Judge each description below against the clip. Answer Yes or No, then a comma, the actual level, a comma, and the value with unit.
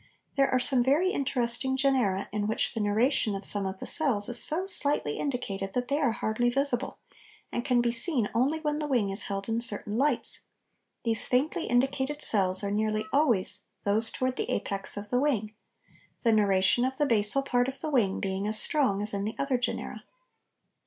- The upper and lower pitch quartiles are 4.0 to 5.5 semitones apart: Yes, average, 4.8 semitones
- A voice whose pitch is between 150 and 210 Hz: No, high, 240 Hz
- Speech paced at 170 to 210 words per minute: Yes, average, 195 wpm